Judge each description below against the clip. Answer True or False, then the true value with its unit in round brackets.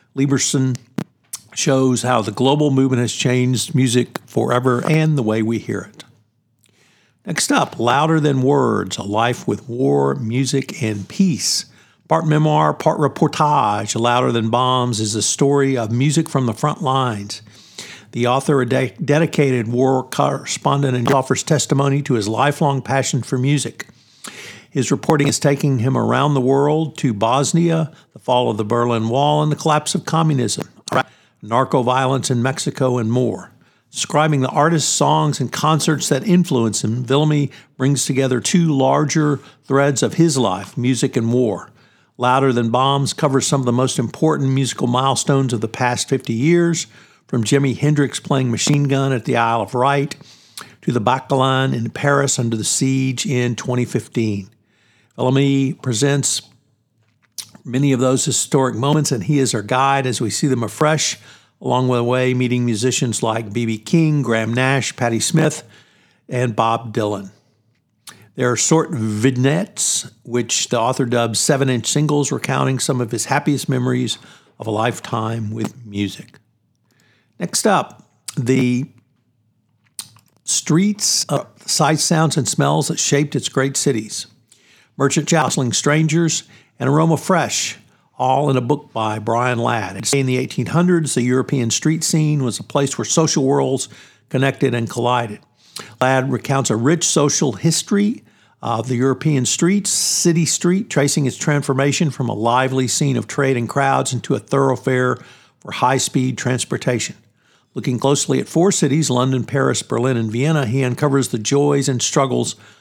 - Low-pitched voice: True (130 Hz)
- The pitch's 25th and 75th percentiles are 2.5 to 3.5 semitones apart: True (3.2 semitones)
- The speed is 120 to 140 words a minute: False (155 wpm)